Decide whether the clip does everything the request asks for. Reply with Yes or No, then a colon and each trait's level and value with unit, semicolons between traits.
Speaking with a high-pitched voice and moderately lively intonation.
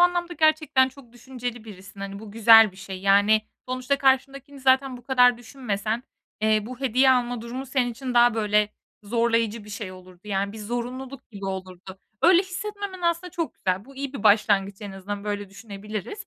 Yes: high, 235 Hz; average, 4.6 semitones